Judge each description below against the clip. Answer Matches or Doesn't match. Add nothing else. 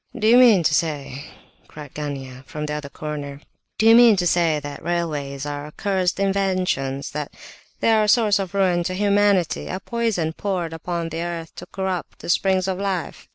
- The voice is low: Doesn't match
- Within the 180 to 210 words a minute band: Matches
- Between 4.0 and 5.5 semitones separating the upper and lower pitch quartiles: Matches